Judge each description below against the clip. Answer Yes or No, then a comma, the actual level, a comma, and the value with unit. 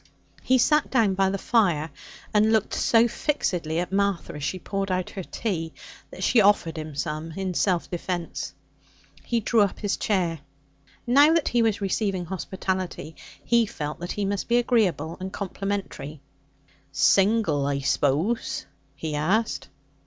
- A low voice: No, high, 190 Hz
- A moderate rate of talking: Yes, average, 150 wpm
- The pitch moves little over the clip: No, average, 4.9 semitones